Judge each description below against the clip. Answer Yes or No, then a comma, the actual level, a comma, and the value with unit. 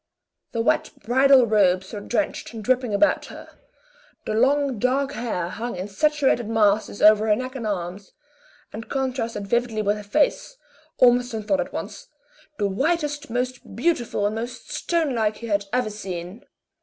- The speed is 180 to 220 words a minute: No, average, 155 wpm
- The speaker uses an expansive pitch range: No, average, 3.9 semitones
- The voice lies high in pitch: Yes, high, 230 Hz